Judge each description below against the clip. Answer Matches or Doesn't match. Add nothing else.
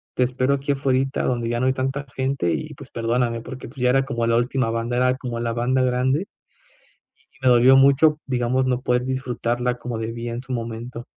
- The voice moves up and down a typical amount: Doesn't match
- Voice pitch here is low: Matches